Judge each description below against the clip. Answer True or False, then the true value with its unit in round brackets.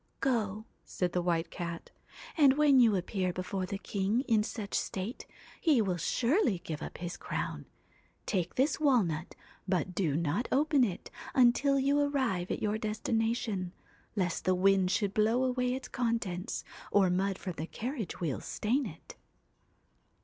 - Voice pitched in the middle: False (210 Hz)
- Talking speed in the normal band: True (160 wpm)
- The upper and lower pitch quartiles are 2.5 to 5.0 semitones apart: False (5.5 semitones)